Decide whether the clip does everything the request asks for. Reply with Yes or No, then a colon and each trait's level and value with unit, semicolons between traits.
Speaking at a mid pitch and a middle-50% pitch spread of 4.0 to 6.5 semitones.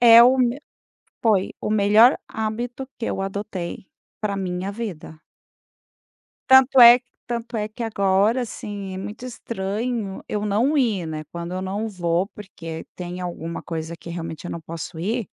No: high, 205 Hz; average, 4.5 semitones